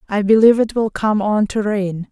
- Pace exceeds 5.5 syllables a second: No, 5.2 syllables/s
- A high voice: Yes, high, 210 Hz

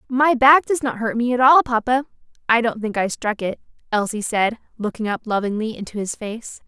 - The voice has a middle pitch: No, high, 235 Hz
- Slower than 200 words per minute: No, fast, 205 wpm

